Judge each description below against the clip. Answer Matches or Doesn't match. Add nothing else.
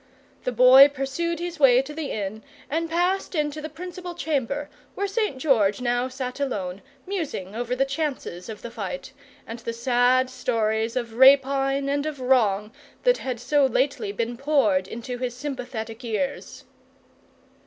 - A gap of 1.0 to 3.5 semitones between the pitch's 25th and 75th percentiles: Doesn't match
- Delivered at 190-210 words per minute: Doesn't match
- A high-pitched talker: Matches